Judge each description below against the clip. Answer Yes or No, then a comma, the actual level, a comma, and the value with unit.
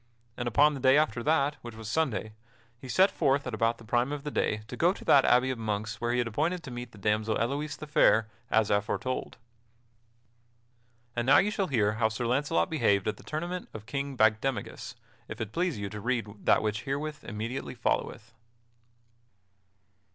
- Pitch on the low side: Yes, low, 120 Hz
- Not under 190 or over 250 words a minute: Yes, average, 195 wpm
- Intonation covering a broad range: No, average, 4.7 semitones